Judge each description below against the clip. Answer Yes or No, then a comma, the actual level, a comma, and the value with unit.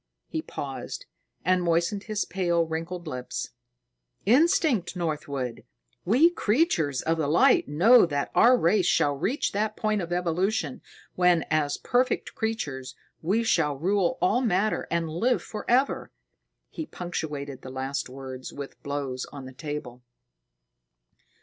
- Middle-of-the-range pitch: Yes, medium, 170 Hz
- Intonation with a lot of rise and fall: Yes, wide, 6.9 semitones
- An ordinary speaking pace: No, slow, 130 wpm